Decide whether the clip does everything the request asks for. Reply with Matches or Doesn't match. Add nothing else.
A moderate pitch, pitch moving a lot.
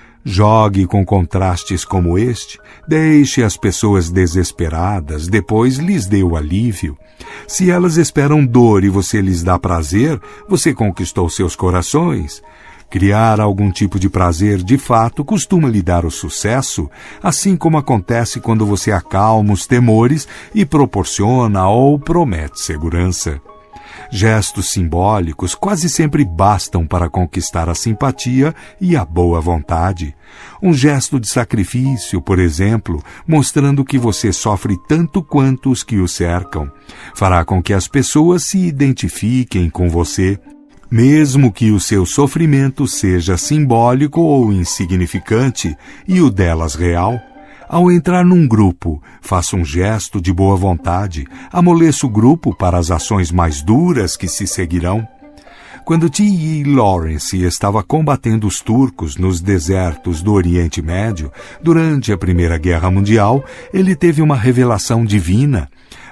Doesn't match